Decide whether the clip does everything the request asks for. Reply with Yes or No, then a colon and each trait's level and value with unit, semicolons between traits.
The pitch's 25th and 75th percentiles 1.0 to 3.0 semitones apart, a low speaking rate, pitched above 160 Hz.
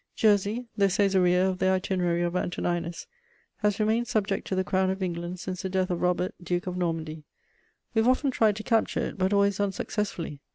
No: narrow, 2.5 semitones; average, 195 wpm; high, 190 Hz